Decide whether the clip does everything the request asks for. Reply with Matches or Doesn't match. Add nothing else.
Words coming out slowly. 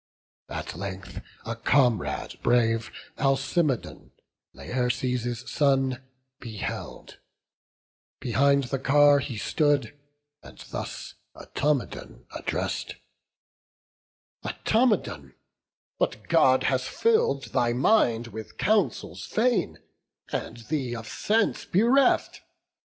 Matches